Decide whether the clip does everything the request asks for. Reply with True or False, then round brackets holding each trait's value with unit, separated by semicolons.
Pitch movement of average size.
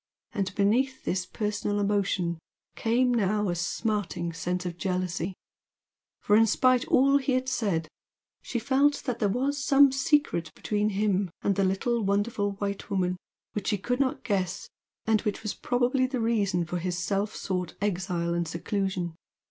True (4.7 semitones)